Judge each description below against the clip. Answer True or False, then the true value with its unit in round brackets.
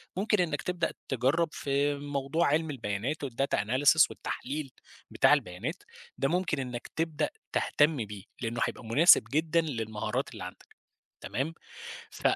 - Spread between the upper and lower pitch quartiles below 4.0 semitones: False (4.5 semitones)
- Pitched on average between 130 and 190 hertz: True (140 Hz)